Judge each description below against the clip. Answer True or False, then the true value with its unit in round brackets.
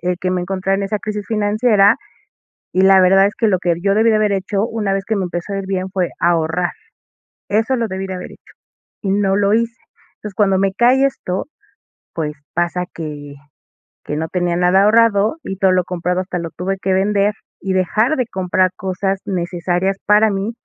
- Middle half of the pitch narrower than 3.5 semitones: True (2.4 semitones)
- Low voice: False (195 Hz)